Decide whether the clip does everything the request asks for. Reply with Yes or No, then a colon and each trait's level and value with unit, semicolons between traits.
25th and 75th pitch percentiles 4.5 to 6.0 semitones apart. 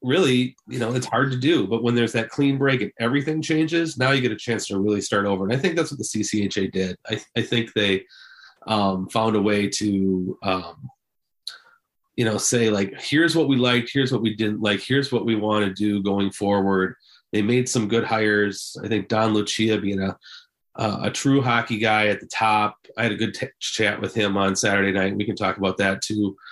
No: average, 3.3 semitones